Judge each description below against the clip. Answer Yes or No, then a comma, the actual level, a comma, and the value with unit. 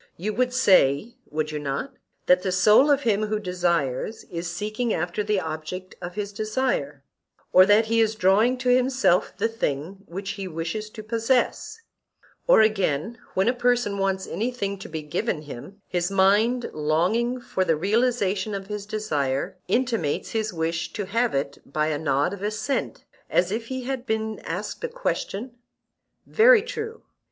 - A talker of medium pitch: No, high, 205 Hz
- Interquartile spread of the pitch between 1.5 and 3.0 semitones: No, average, 5.2 semitones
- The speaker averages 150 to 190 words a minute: Yes, average, 165 wpm